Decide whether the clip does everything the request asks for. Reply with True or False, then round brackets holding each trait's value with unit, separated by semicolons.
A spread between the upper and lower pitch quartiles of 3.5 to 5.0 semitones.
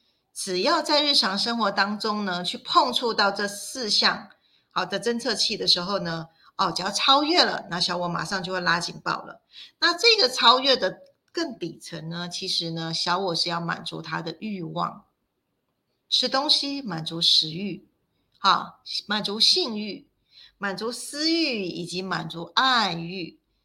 False (5.6 semitones)